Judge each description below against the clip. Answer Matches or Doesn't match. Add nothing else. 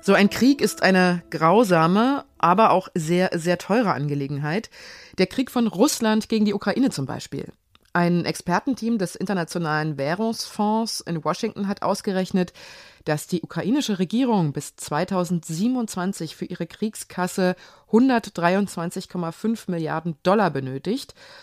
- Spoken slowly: Matches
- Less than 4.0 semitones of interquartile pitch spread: Doesn't match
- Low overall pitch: Doesn't match